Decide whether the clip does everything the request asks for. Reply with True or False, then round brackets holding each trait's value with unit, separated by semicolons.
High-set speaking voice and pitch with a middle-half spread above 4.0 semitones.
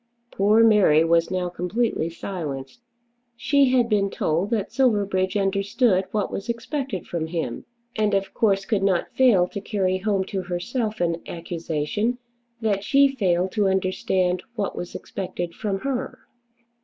False (195 Hz; 3.7 semitones)